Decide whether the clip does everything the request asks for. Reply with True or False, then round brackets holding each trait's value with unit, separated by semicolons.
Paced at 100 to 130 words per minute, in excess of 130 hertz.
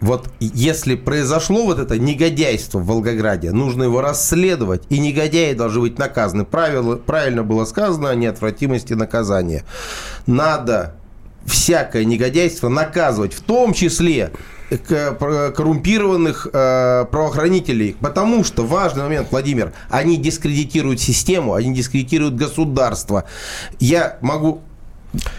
True (110 wpm; 140 Hz)